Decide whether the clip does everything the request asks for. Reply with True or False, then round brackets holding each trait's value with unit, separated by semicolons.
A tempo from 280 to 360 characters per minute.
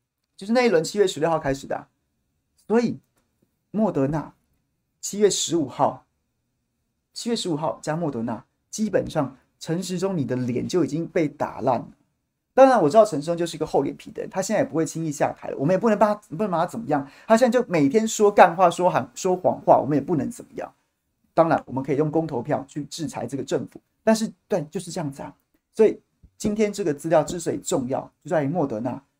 True (325 characters per minute)